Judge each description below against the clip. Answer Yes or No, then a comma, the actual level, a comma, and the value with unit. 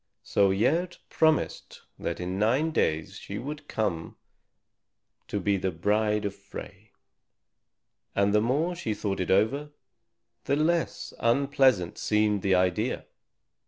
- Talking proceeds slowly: Yes, slow, 125 wpm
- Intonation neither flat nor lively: No, wide, 6.3 semitones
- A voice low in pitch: Yes, low, 105 Hz